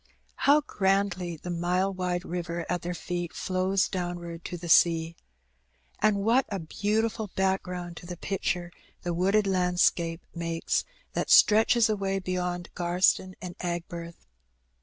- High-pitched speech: No, medium, 180 Hz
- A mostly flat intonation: Yes, narrow, 2.0 semitones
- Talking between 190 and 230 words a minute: No, slow, 135 wpm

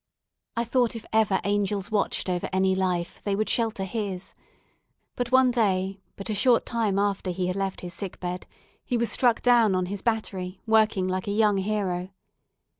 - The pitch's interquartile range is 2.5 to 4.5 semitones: Yes, average, 3.0 semitones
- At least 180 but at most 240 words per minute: Yes, average, 185 wpm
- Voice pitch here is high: Yes, high, 200 Hz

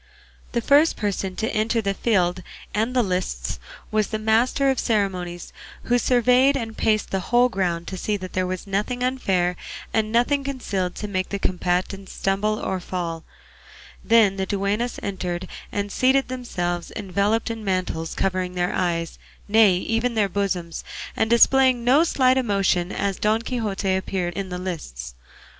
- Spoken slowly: No, average, 160 wpm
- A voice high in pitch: Yes, high, 200 Hz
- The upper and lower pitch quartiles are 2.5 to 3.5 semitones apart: No, average, 4.0 semitones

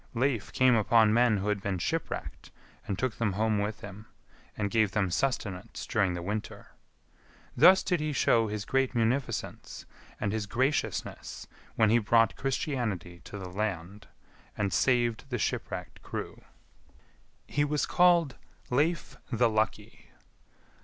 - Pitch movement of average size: Yes, average, 4.1 semitones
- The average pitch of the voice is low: Yes, low, 110 Hz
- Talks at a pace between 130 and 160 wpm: Yes, average, 140 wpm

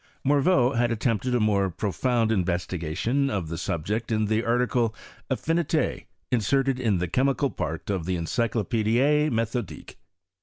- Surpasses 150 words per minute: No, average, 145 wpm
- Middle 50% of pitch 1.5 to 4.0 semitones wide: No, average, 4.9 semitones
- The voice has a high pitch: No, low, 115 Hz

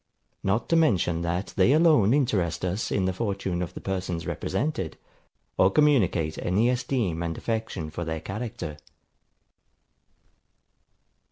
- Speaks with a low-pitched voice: Yes, very low, 95 Hz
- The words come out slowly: Yes, slow, 125 wpm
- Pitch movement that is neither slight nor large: No, wide, 5.7 semitones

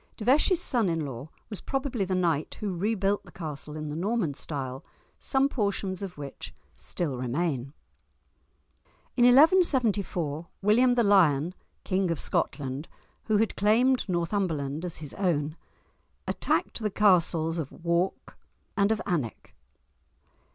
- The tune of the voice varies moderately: No, wide, 5.7 semitones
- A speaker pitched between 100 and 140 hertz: No, medium, 180 Hz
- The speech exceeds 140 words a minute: No, slow, 135 wpm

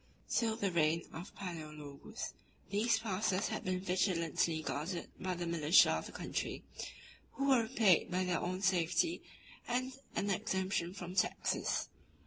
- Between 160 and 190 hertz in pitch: Yes, medium, 185 Hz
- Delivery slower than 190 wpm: Yes, average, 140 wpm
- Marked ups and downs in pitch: No, average, 3.3 semitones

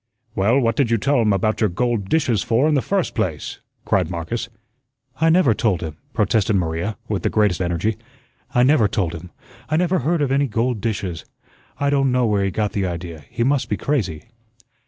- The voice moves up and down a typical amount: No, wide, 5.9 semitones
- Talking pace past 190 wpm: Yes, average, 200 wpm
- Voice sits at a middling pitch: No, low, 110 Hz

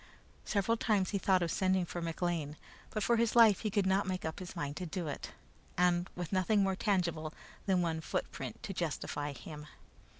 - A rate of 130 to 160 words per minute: No, average, 190 wpm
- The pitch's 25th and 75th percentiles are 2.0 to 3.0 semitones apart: No, average, 3.7 semitones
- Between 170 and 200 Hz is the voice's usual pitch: Yes, medium, 185 Hz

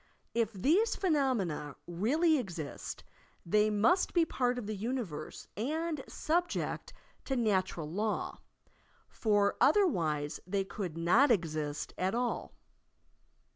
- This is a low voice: No, high, 215 Hz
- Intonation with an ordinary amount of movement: No, wide, 7.7 semitones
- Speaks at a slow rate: Yes, slow, 110 wpm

